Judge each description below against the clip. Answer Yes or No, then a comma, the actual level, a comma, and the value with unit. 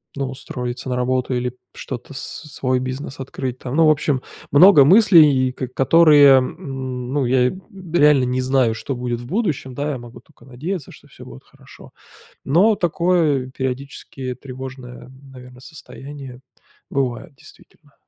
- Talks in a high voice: No, low, 130 Hz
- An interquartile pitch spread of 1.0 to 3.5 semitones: Yes, average, 2.7 semitones